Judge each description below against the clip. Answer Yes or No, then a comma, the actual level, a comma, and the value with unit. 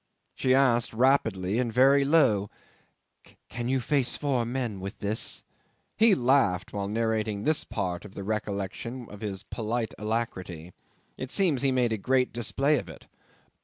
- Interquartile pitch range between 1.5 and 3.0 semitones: No, average, 4.3 semitones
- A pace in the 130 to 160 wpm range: Yes, average, 155 wpm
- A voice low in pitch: Yes, low, 115 Hz